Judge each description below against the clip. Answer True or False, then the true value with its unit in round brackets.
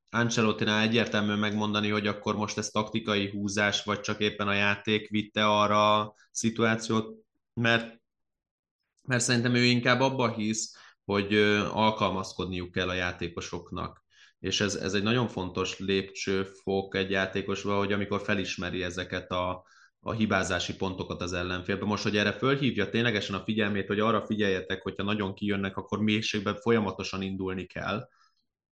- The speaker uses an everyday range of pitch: False (2.1 semitones)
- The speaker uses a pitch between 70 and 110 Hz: True (105 Hz)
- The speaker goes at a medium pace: True (140 wpm)